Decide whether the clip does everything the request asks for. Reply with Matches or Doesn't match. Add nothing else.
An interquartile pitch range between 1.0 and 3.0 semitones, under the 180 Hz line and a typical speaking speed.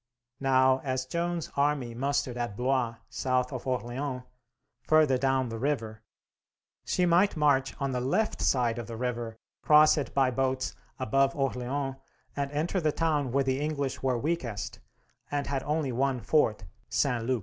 Matches